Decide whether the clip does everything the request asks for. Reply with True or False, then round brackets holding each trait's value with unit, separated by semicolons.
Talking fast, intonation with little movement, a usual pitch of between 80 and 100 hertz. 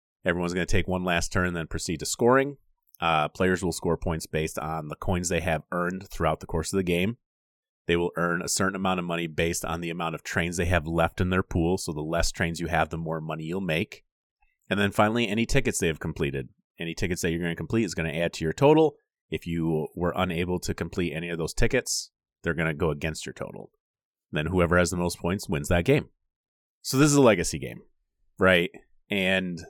True (240 wpm; 2.2 semitones; 85 Hz)